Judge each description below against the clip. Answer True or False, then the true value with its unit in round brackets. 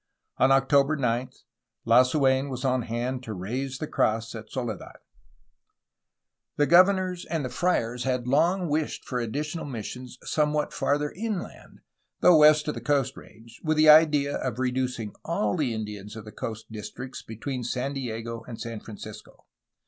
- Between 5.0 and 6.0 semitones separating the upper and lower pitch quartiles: False (4.4 semitones)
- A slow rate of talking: False (155 wpm)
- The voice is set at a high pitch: False (130 Hz)